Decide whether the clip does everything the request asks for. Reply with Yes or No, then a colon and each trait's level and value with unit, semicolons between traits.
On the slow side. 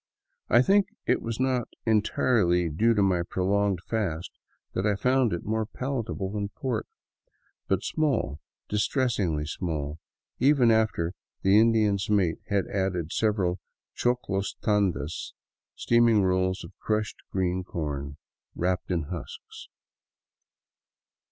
Yes: slow, 120 wpm